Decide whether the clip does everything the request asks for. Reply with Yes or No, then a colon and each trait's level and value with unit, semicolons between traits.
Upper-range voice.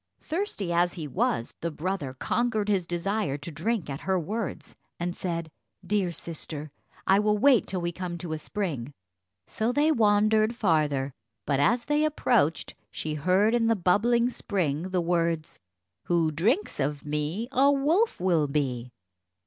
No: medium, 180 Hz